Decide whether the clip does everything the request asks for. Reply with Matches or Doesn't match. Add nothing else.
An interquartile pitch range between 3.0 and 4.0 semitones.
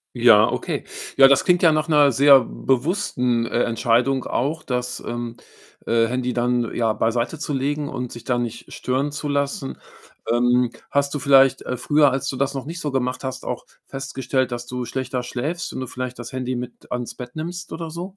Doesn't match